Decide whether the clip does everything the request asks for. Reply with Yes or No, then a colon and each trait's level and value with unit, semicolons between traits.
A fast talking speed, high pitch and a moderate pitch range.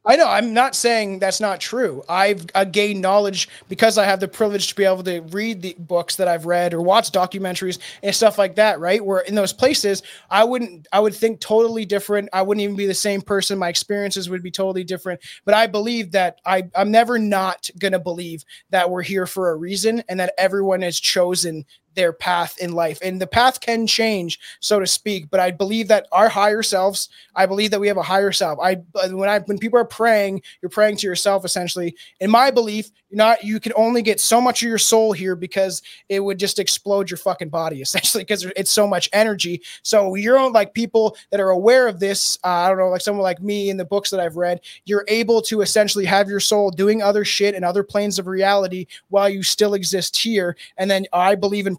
No: fast, 230 wpm; high, 195 Hz; narrow, 2.3 semitones